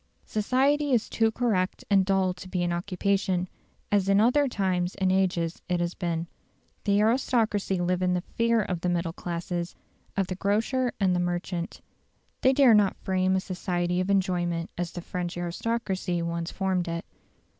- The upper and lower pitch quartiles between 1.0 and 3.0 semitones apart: Yes, average, 2.7 semitones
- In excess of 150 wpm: Yes, average, 170 wpm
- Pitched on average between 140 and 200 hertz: Yes, medium, 185 Hz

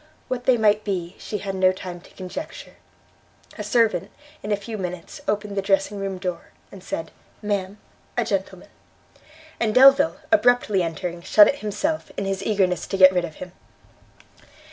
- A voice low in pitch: No, high, 195 Hz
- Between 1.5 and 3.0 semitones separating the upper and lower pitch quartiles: Yes, narrow, 2.6 semitones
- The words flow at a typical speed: Yes, average, 165 wpm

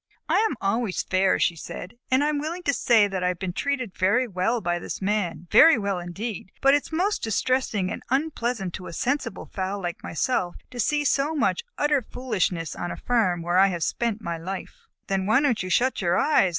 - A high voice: Yes, high, 210 Hz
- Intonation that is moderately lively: No, wide, 6.2 semitones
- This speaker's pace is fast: Yes, fast, 225 wpm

